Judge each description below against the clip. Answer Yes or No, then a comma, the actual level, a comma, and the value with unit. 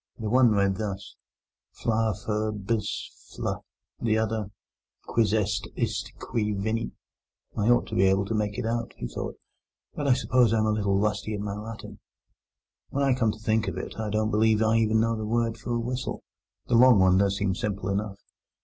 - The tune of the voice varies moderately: No, narrow, 1.9 semitones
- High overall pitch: No, low, 110 Hz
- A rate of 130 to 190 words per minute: No, average, 200 wpm